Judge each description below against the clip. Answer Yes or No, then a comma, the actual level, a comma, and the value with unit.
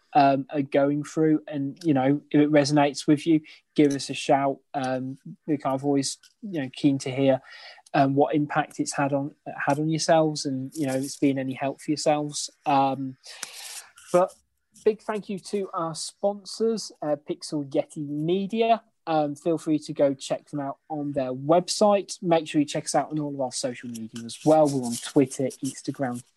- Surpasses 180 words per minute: Yes, average, 190 wpm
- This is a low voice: No, medium, 145 Hz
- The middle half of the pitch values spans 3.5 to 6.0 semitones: No, average, 2.7 semitones